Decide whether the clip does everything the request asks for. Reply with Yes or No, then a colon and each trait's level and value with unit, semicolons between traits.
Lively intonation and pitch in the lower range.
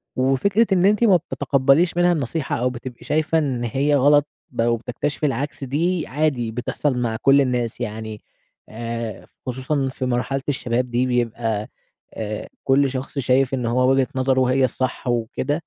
No: average, 3.2 semitones; low, 130 Hz